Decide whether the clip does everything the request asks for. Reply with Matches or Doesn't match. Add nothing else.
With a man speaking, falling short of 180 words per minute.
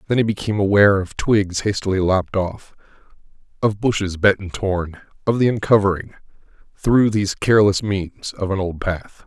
Matches